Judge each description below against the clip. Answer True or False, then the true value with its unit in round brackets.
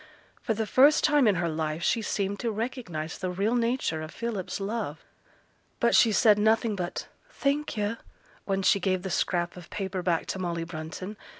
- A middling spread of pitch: True (4.5 semitones)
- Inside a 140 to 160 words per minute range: False (185 wpm)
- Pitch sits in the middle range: False (195 Hz)